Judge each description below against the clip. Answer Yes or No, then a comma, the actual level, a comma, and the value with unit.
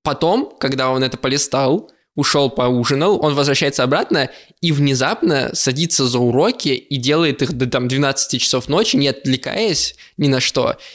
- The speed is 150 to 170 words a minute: Yes, average, 155 wpm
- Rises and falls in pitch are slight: Yes, narrow, 1.6 semitones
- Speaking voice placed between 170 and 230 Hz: No, low, 135 Hz